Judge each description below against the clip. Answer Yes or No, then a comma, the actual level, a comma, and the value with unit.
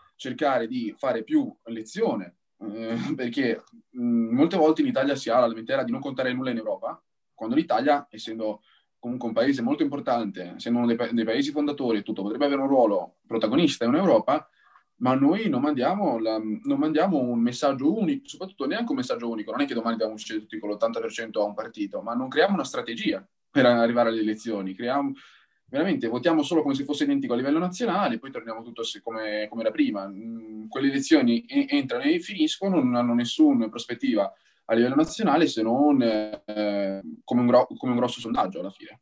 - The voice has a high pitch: No, medium, 140 Hz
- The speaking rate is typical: No, fast, 190 wpm